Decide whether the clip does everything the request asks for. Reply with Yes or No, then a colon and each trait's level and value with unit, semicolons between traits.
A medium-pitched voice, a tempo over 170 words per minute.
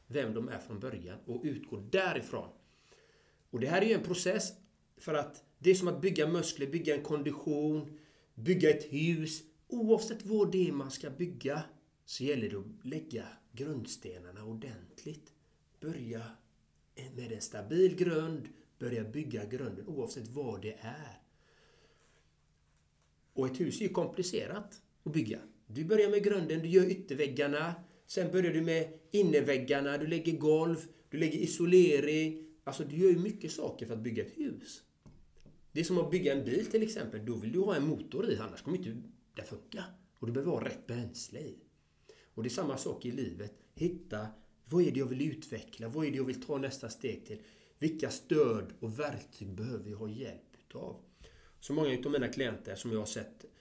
Yes: medium, 150 Hz; average, 180 wpm